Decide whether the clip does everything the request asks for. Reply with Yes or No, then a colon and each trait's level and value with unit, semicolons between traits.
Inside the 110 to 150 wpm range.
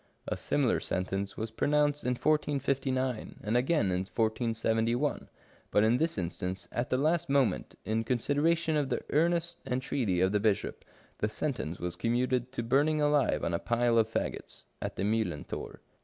No: average, 165 wpm